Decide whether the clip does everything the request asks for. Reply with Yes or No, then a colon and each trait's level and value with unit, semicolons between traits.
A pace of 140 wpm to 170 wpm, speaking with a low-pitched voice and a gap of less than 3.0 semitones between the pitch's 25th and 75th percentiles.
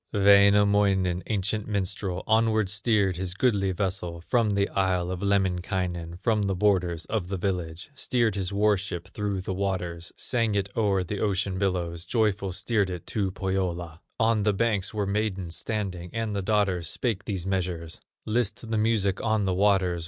Yes: average, 165 wpm; low, 100 Hz; narrow, 2.4 semitones